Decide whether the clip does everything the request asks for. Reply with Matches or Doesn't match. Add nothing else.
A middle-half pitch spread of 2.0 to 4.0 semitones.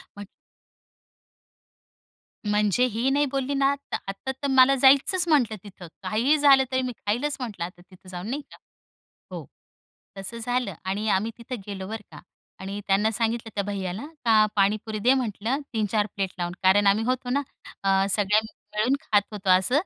Doesn't match